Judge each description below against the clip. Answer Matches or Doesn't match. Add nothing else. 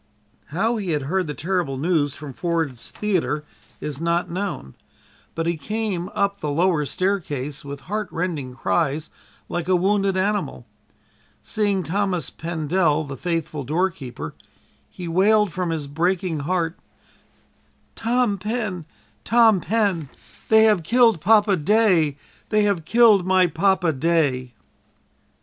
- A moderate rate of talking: Doesn't match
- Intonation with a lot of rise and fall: Doesn't match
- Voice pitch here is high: Doesn't match